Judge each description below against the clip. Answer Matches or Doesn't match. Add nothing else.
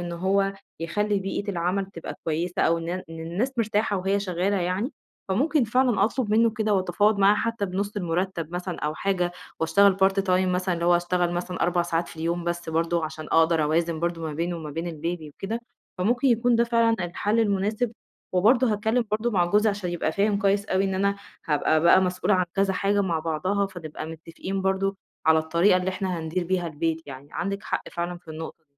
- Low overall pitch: Doesn't match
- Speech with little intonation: Doesn't match